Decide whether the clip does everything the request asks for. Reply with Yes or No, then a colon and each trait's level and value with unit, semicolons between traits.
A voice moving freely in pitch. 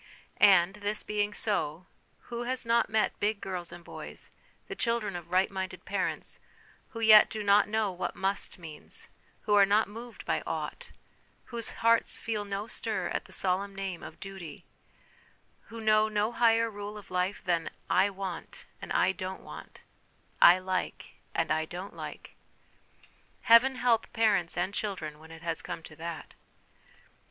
No: average, 3.1 semitones